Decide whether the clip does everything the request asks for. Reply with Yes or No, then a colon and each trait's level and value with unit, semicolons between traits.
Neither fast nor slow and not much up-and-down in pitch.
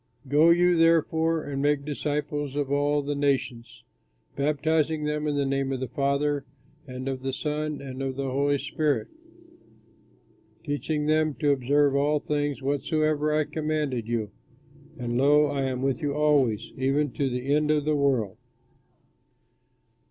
Yes: average, 150 wpm; narrow, 1.9 semitones